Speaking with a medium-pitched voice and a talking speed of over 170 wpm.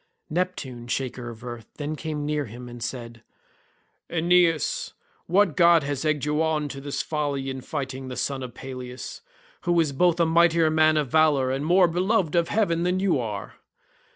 Yes: medium, 150 Hz; average, 185 wpm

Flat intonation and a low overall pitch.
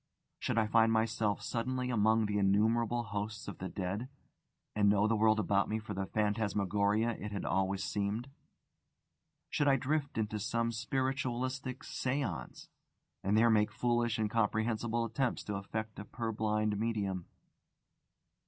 Yes: narrow, 2.3 semitones; low, 110 Hz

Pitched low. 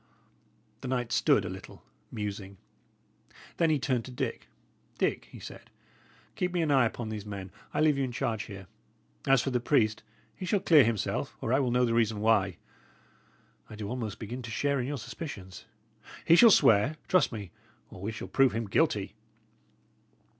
Yes: low, 120 Hz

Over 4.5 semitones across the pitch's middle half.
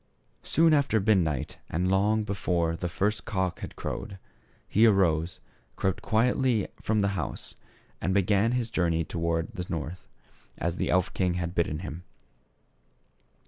No: average, 3.9 semitones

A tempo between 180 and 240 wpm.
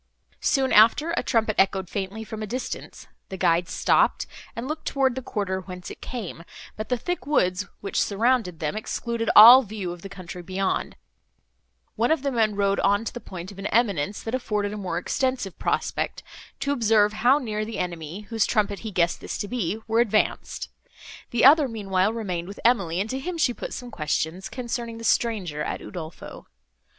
Yes: average, 190 wpm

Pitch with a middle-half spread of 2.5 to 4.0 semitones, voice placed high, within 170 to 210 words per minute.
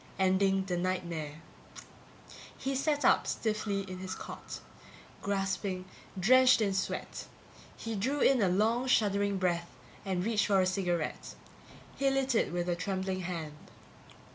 No: average, 3.1 semitones; high, 195 Hz; average, 140 wpm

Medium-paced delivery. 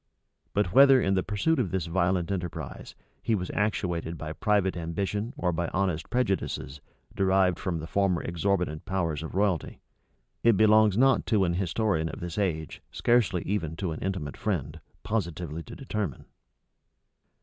Yes: average, 155 wpm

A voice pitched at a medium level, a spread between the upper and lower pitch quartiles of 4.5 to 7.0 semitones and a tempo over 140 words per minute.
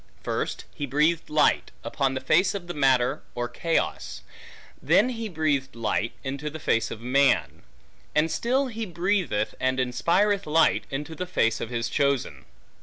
Yes: medium, 150 Hz; average, 5.1 semitones; average, 160 wpm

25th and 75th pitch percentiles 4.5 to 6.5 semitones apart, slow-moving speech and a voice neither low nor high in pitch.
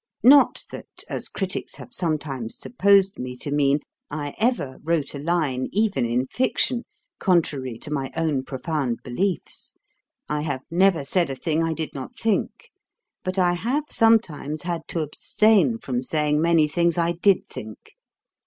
No: average, 5.2 semitones; average, 155 wpm; medium, 160 Hz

